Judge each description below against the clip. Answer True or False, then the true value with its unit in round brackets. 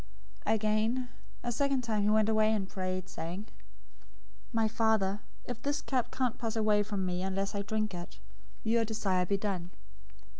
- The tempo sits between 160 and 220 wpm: True (165 wpm)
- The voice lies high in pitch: True (215 Hz)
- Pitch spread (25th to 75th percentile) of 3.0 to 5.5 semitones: False (2.5 semitones)